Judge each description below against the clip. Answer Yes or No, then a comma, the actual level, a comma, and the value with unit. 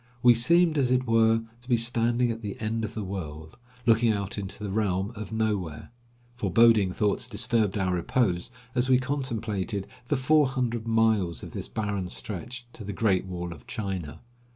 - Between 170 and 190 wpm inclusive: Yes, average, 175 wpm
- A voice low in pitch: Yes, low, 110 Hz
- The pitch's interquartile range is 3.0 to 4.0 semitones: Yes, average, 3.6 semitones